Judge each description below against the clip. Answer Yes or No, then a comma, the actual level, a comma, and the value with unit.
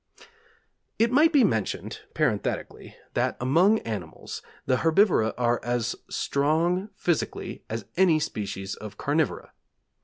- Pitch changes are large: Yes, wide, 8.2 semitones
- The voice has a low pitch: No, medium, 145 Hz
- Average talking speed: No, slow, 115 wpm